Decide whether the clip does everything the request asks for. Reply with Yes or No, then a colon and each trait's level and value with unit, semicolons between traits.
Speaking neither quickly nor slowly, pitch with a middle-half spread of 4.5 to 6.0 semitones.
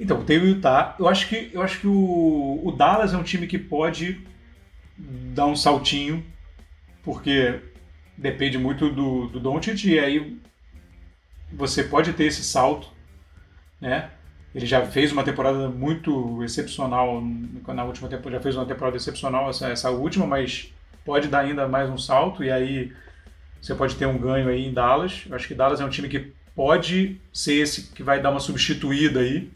No: average, 175 wpm; average, 3.7 semitones